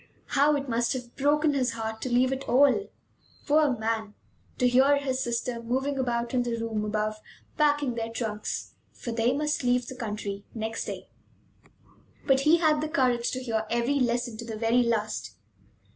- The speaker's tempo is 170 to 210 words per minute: Yes, average, 175 wpm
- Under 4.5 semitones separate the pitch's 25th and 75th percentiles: Yes, average, 3.1 semitones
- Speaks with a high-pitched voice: Yes, high, 245 Hz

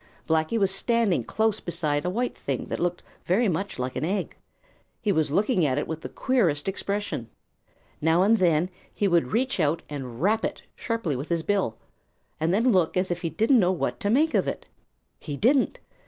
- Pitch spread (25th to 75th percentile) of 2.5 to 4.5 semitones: No, wide, 5.4 semitones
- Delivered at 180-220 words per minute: Yes, average, 200 wpm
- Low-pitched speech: No, medium, 180 Hz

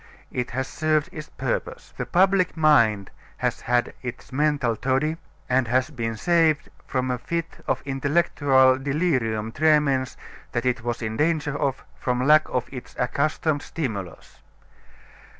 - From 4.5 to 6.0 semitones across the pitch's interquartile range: No, average, 3.9 semitones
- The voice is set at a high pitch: No, low, 135 Hz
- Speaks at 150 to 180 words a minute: No, average, 140 wpm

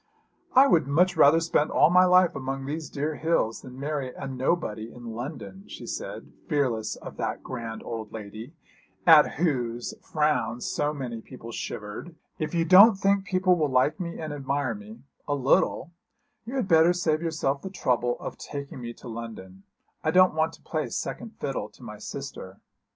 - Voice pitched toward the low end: No, medium, 145 Hz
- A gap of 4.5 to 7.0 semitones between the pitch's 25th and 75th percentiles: Yes, wide, 5.6 semitones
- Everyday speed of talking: Yes, average, 180 wpm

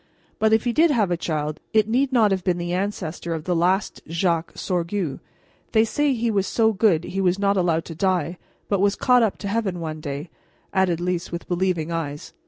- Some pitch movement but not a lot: Yes, average, 4.0 semitones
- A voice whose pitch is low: No, medium, 185 Hz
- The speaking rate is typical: No, fast, 210 wpm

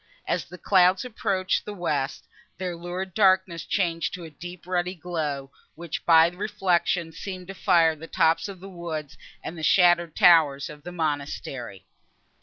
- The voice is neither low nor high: Yes, medium, 175 Hz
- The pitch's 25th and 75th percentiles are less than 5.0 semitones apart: Yes, narrow, 2.4 semitones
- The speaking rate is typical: Yes, average, 160 wpm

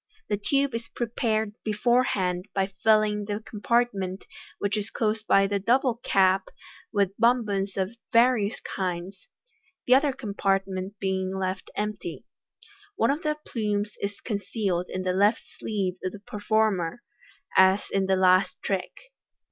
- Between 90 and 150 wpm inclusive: Yes, average, 140 wpm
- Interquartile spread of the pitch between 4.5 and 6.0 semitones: No, average, 2.8 semitones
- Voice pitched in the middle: No, high, 205 Hz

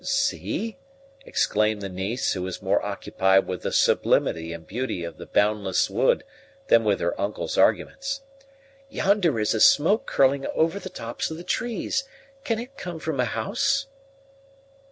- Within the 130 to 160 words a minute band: Yes, average, 155 wpm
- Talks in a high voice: No, low, 130 Hz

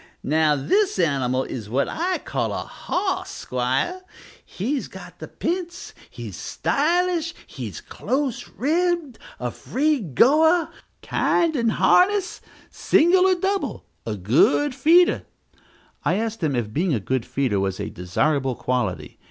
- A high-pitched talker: Yes, very high, 250 Hz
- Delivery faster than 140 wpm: No, slow, 135 wpm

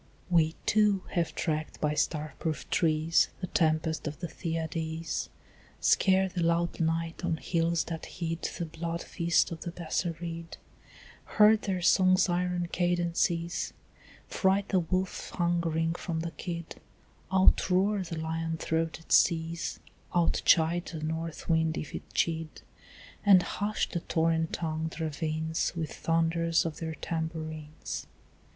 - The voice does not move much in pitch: Yes, narrow, 1.4 semitones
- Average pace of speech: No, slow, 130 wpm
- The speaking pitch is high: No, medium, 165 Hz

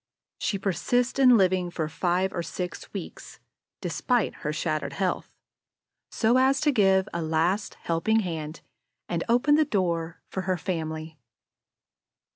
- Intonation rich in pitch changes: No, average, 5.0 semitones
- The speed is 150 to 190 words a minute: No, slow, 135 wpm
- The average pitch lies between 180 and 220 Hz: Yes, medium, 185 Hz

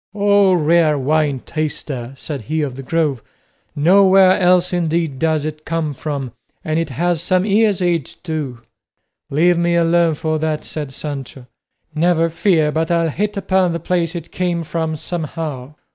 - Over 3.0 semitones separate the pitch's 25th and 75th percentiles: No, average, 2.7 semitones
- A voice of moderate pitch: Yes, medium, 160 Hz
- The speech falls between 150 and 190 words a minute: Yes, average, 160 wpm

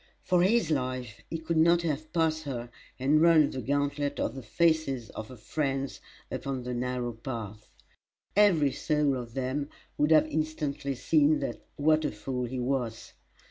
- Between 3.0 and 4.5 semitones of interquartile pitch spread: Yes, average, 3.7 semitones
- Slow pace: No, average, 160 wpm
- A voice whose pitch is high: No, medium, 140 Hz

